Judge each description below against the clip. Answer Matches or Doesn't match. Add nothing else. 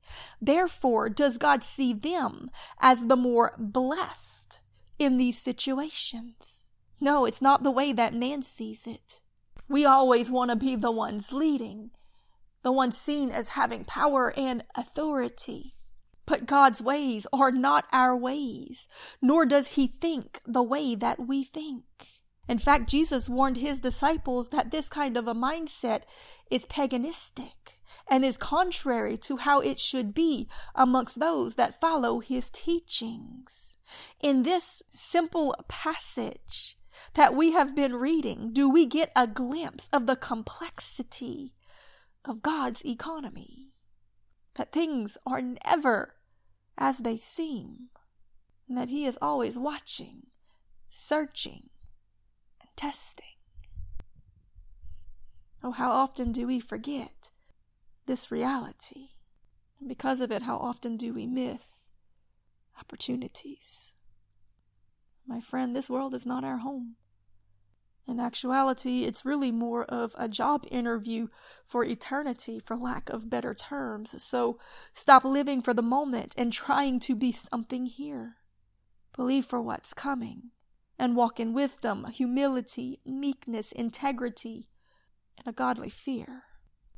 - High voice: Matches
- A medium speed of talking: Doesn't match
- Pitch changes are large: Doesn't match